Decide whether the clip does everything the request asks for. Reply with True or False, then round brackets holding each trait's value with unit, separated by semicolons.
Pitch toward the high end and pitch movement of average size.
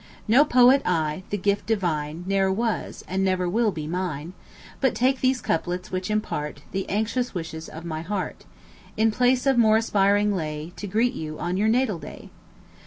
True (195 Hz; 4.7 semitones)